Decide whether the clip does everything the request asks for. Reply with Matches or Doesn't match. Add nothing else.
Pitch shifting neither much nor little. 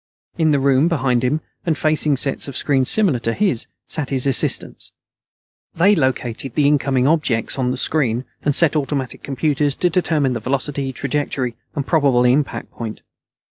Matches